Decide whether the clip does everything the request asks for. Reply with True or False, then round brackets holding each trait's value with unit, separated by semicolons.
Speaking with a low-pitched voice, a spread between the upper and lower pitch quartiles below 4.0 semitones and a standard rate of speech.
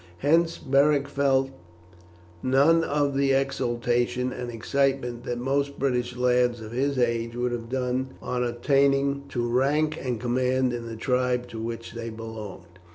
True (125 Hz; 2.5 semitones; 150 wpm)